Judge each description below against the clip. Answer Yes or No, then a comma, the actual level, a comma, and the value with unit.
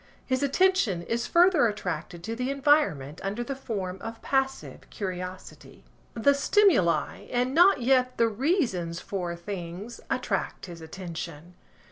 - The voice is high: Yes, high, 225 Hz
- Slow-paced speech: Yes, slow, 130 wpm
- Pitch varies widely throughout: Yes, wide, 7.0 semitones